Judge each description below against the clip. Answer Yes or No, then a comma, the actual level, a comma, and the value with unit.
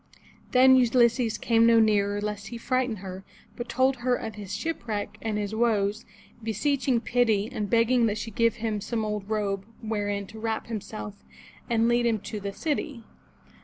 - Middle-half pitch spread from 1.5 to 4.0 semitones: Yes, narrow, 2.4 semitones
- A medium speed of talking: Yes, average, 170 wpm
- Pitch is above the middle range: Yes, high, 225 Hz